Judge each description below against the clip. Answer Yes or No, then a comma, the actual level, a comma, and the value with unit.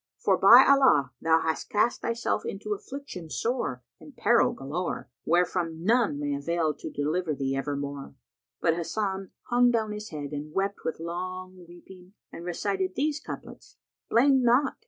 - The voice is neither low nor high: Yes, medium, 180 Hz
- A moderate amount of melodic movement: No, wide, 6.3 semitones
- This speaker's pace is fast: No, average, 155 wpm